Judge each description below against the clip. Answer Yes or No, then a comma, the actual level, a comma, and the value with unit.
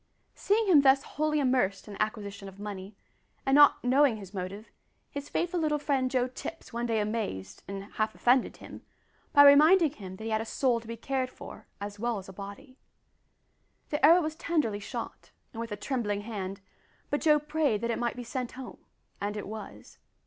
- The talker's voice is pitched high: Yes, high, 235 Hz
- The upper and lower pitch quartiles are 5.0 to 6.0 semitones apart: Yes, wide, 5.5 semitones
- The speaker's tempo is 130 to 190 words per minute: No, average, 200 wpm